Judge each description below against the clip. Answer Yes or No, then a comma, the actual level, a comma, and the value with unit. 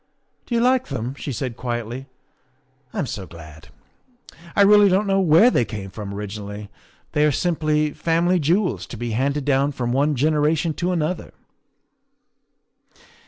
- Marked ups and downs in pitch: Yes, wide, 6.4 semitones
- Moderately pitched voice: Yes, medium, 145 Hz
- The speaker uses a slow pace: No, average, 165 wpm